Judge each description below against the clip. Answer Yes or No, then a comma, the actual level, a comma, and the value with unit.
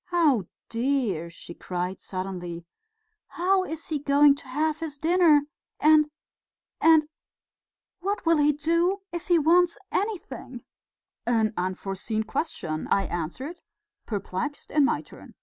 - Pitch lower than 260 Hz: No, very high, 290 Hz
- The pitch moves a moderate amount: No, wide, 8.8 semitones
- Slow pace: Yes, slow, 125 wpm